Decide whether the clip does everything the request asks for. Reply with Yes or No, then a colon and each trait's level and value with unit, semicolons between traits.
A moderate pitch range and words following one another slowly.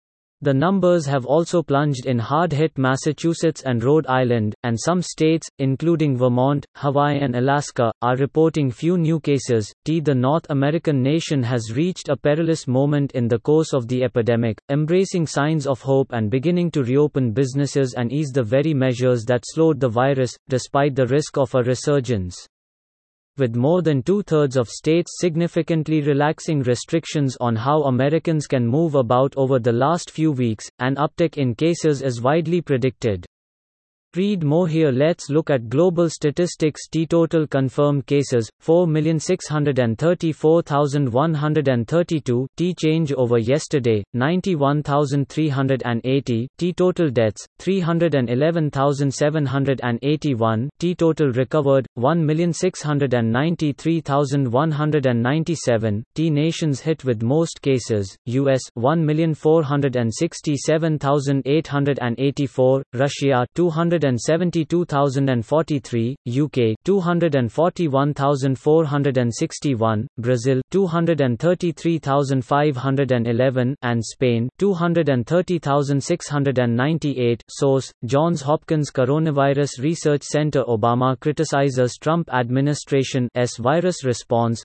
Yes: average, 3.8 semitones; slow, 105 wpm